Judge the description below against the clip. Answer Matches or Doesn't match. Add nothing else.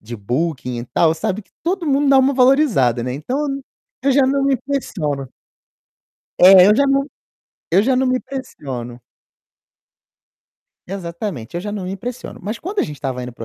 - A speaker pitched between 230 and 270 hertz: Doesn't match